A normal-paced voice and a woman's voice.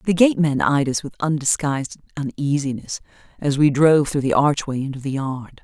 Yes: average, 170 wpm; female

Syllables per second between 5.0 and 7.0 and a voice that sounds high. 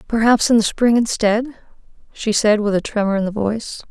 Yes: 5.5 syllables/s; high, 220 Hz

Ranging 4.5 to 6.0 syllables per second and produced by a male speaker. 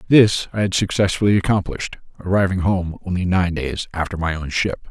Yes: 5.5 syllables/s; male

